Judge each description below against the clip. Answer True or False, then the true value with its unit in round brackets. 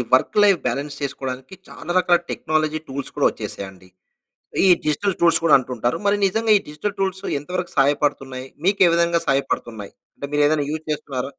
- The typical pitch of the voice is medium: True (150 Hz)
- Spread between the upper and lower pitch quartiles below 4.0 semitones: False (4.7 semitones)